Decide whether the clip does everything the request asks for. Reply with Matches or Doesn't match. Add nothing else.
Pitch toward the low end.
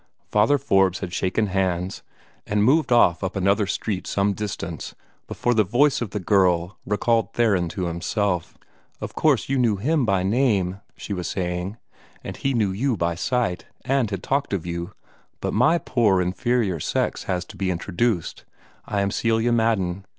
Matches